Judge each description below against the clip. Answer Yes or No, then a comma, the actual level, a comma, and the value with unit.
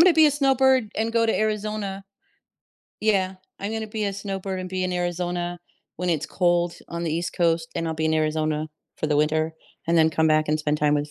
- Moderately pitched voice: Yes, medium, 175 Hz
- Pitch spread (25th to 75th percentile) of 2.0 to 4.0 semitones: No, average, 5.0 semitones